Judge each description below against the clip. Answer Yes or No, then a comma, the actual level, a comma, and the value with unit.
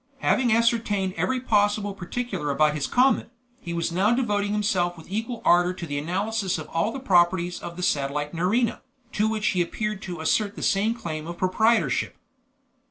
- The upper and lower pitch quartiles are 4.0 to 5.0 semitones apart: Yes, average, 4.3 semitones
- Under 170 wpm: No, average, 175 wpm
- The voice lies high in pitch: Yes, high, 195 Hz